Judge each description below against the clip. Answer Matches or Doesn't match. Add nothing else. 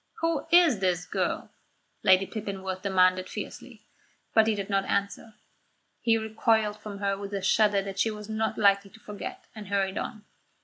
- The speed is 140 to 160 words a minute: Doesn't match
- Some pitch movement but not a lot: Doesn't match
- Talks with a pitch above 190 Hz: Matches